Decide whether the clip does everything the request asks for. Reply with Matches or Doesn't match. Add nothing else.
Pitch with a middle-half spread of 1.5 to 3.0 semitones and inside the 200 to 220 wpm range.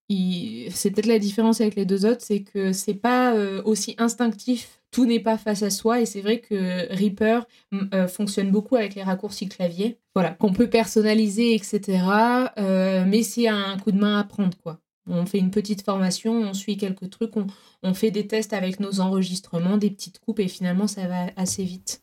Doesn't match